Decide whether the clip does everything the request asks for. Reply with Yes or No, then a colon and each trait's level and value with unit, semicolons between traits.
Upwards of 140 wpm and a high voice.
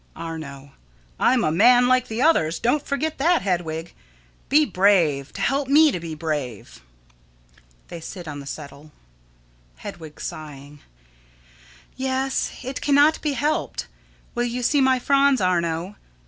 No: slow, 135 wpm; high, 200 Hz